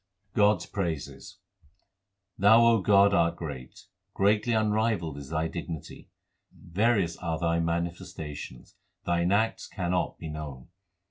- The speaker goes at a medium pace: No, slow, 120 wpm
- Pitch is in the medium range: No, very low, 85 Hz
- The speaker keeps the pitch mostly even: No, average, 4.4 semitones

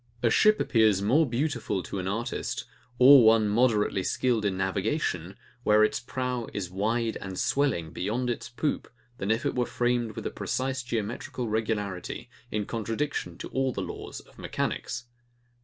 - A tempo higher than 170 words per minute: No, average, 160 wpm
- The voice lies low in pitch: Yes, low, 115 Hz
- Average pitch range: Yes, average, 3.7 semitones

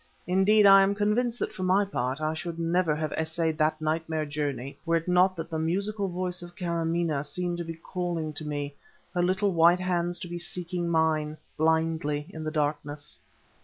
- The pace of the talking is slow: No, average, 190 wpm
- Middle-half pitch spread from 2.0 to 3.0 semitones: Yes, narrow, 2.6 semitones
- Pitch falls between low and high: Yes, medium, 165 Hz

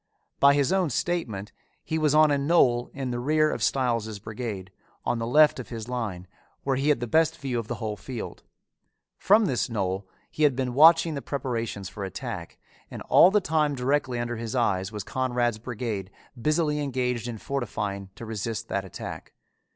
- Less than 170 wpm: No, average, 185 wpm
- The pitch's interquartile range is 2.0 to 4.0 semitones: No, average, 4.7 semitones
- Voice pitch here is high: No, low, 125 Hz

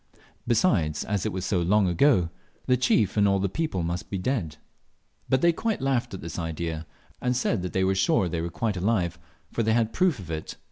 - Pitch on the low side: Yes, very low, 95 Hz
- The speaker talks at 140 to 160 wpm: No, fast, 205 wpm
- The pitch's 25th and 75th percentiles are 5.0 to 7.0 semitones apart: Yes, wide, 5.6 semitones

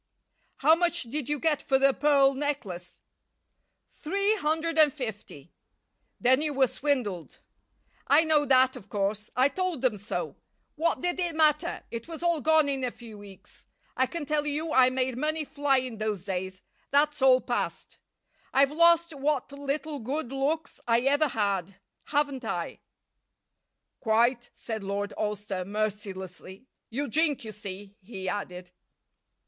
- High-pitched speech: Yes, very high, 265 Hz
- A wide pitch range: Yes, wide, 6.2 semitones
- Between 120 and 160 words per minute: Yes, average, 150 wpm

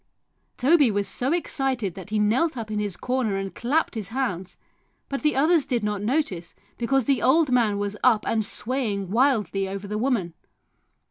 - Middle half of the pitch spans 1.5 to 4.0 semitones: No, average, 4.8 semitones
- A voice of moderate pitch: No, high, 230 Hz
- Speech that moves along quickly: No, average, 180 wpm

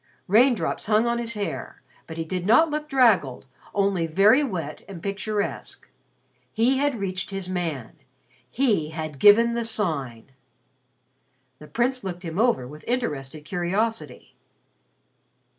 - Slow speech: Yes, slow, 130 wpm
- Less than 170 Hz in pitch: No, high, 195 Hz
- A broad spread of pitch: Yes, wide, 6.3 semitones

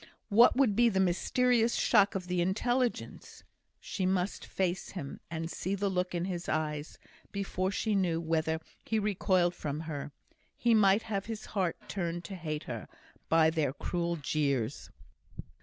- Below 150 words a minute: No, average, 155 wpm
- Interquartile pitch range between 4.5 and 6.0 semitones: No, average, 3.7 semitones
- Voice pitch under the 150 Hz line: No, medium, 180 Hz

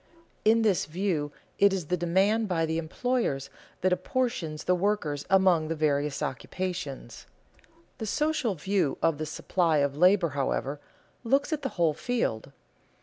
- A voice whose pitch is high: No, medium, 180 Hz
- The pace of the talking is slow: No, average, 145 wpm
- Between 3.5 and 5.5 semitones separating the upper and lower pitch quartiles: Yes, average, 5.2 semitones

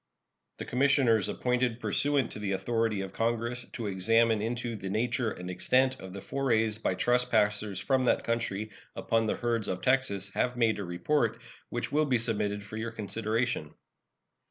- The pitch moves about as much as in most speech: Yes, average, 3.1 semitones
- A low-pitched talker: Yes, low, 115 Hz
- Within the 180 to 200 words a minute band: No, average, 165 wpm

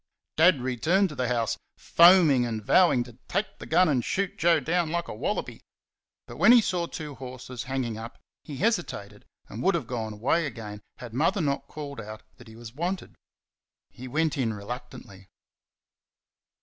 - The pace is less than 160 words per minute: No, average, 175 wpm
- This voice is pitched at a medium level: No, low, 130 Hz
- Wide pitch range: Yes, wide, 6.4 semitones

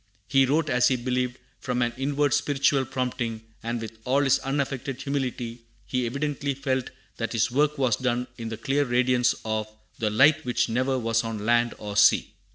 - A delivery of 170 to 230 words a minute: Yes, average, 180 wpm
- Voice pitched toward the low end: Yes, low, 125 Hz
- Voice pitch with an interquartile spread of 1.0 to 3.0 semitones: Yes, average, 2.7 semitones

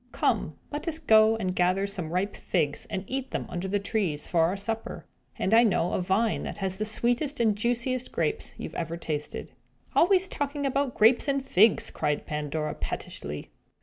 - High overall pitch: Yes, high, 210 Hz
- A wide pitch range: Yes, wide, 5.9 semitones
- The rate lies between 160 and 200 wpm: Yes, average, 180 wpm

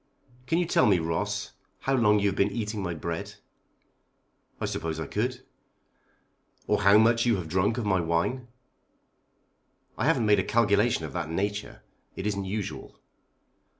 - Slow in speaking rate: No, average, 160 wpm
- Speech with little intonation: No, average, 4.7 semitones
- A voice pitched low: Yes, low, 100 Hz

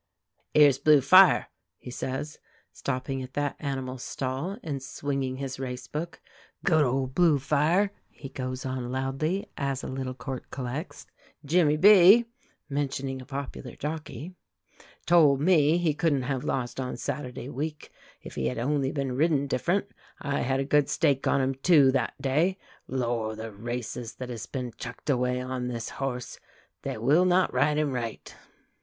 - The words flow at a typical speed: Yes, average, 160 wpm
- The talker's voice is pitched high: No, low, 135 Hz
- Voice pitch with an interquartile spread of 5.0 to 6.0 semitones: No, average, 2.9 semitones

